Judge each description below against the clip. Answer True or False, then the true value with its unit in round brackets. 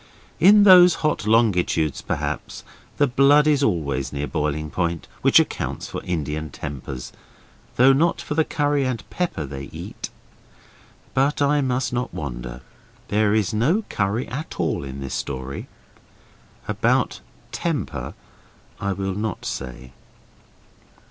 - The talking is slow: True (130 wpm)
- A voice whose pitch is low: True (105 Hz)